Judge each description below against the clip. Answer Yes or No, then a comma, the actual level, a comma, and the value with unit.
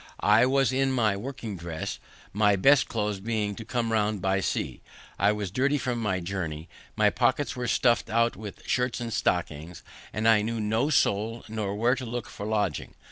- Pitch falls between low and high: No, low, 110 Hz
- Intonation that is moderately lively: Yes, average, 3.3 semitones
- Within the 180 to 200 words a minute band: Yes, average, 190 wpm